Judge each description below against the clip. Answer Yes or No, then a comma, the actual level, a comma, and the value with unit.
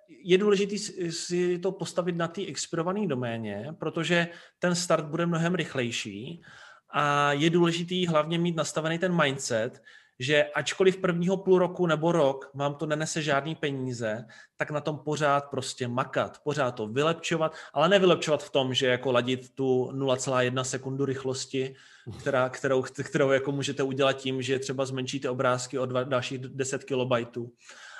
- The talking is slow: No, average, 150 wpm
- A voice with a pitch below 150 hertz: Yes, medium, 140 Hz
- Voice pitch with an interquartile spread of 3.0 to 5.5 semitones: Yes, average, 4.4 semitones